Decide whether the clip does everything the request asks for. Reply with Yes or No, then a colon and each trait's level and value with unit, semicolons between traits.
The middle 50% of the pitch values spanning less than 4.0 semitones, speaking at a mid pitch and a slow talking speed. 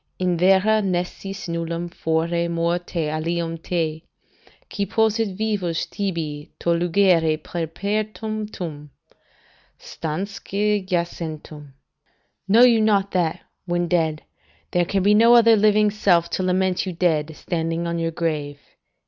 Yes: average, 3.4 semitones; medium, 175 Hz; slow, 120 wpm